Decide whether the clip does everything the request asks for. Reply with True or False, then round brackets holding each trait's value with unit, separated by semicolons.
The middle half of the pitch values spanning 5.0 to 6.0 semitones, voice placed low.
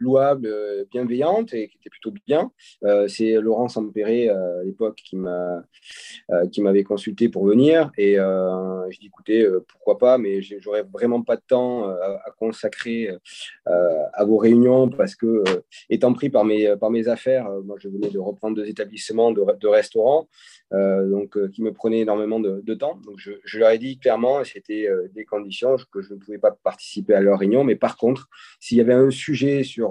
False (3.5 semitones; 110 Hz)